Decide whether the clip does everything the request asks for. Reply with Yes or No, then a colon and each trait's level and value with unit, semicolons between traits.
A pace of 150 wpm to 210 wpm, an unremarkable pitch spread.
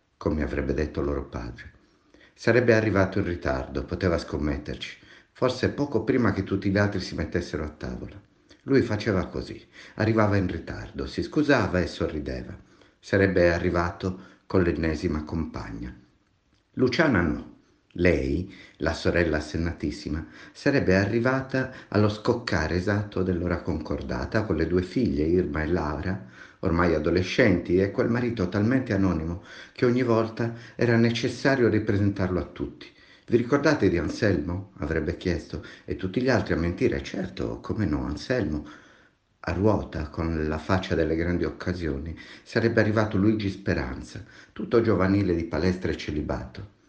No: average, 135 wpm; average, 4.7 semitones